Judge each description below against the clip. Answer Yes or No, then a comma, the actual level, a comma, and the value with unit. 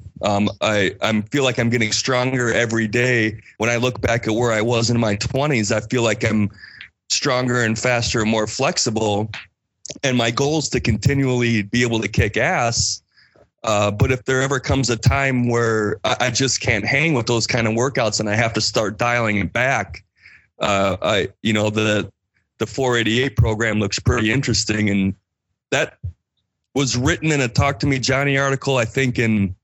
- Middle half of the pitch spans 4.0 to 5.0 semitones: No, average, 3.1 semitones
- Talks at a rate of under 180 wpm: No, average, 190 wpm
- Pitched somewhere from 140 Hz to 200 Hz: No, low, 115 Hz